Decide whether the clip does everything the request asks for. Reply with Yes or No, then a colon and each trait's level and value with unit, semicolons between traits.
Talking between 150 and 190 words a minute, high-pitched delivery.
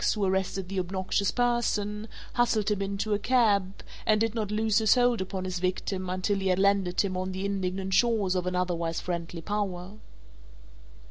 Yes: average, 180 wpm; high, 195 Hz